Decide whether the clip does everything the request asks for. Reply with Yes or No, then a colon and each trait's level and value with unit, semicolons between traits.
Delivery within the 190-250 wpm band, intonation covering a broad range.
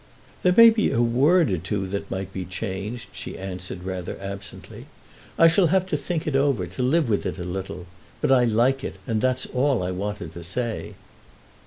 Yes: average, 200 wpm; wide, 6.5 semitones